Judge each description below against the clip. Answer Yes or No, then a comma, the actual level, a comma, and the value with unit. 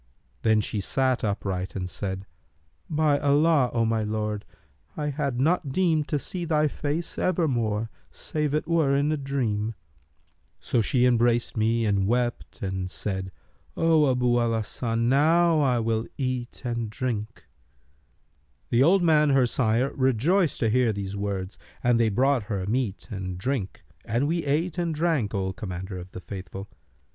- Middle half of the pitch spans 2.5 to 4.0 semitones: No, wide, 5.6 semitones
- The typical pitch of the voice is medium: No, low, 120 Hz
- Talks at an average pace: Yes, average, 160 wpm